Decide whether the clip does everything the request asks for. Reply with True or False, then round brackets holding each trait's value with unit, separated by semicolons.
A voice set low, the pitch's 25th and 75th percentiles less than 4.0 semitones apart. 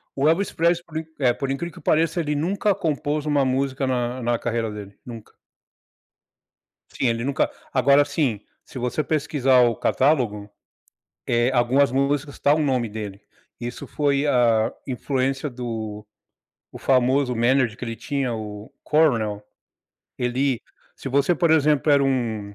True (130 Hz; 3.5 semitones)